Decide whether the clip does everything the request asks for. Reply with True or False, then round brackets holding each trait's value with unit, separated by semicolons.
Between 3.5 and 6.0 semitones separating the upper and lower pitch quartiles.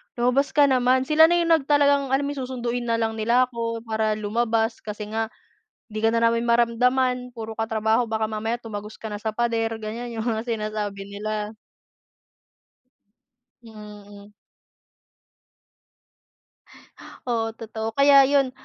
False (2.4 semitones)